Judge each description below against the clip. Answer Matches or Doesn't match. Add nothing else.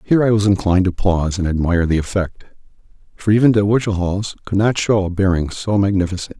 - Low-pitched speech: Matches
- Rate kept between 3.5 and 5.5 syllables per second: Doesn't match